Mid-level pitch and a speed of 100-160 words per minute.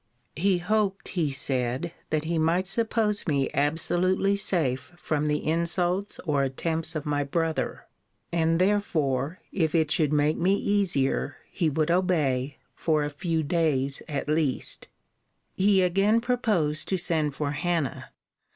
Yes: medium, 160 Hz; average, 140 wpm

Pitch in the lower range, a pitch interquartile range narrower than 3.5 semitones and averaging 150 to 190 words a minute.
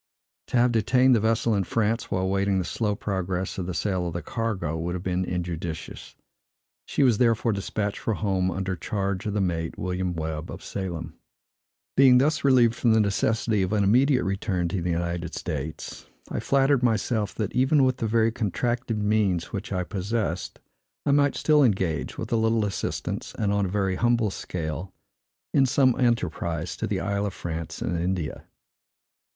No: low, 100 Hz; average, 4.3 semitones; average, 180 wpm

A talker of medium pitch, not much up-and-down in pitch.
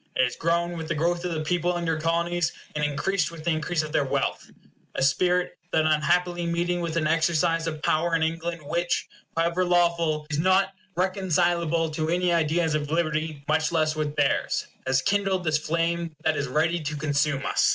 Yes: medium, 165 Hz; narrow, 2.0 semitones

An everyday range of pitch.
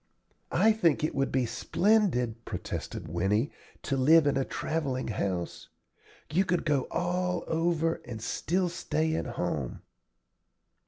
No: wide, 6.0 semitones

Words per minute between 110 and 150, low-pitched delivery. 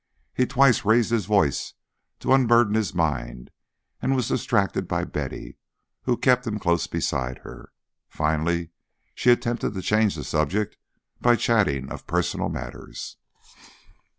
Yes: slow, 135 wpm; low, 105 Hz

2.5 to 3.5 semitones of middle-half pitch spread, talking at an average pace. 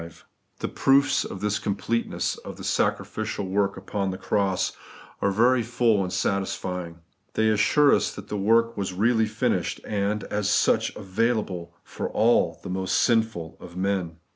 Yes: average, 2.9 semitones; average, 150 wpm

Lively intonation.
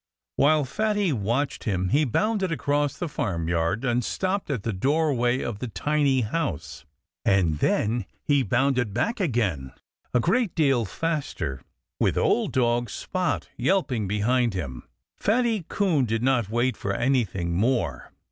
Yes: wide, 6.7 semitones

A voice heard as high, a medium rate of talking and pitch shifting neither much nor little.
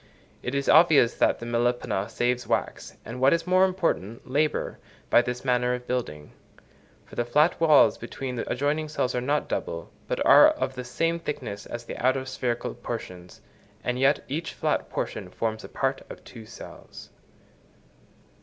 No: low, 125 Hz; average, 170 wpm; average, 3.9 semitones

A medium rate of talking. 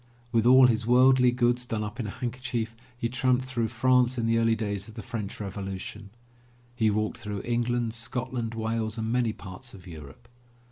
Yes: average, 185 wpm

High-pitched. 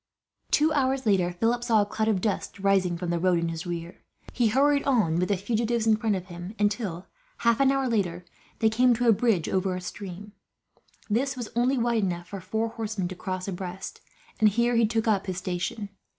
Yes: high, 210 Hz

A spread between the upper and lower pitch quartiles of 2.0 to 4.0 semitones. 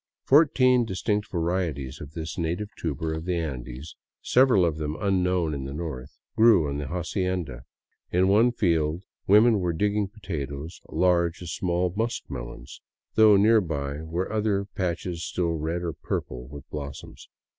No: average, 4.6 semitones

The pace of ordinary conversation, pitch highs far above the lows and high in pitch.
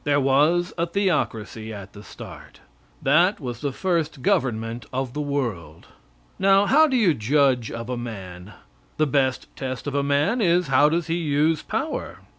No: average, 170 wpm; wide, 5.9 semitones; medium, 140 Hz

